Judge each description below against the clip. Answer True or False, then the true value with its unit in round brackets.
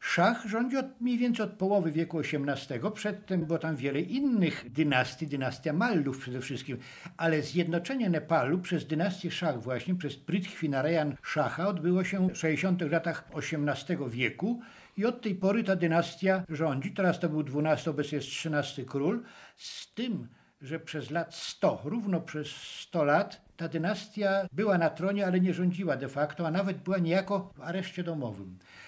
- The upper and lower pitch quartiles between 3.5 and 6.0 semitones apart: True (4.5 semitones)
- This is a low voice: False (170 Hz)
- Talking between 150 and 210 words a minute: True (160 wpm)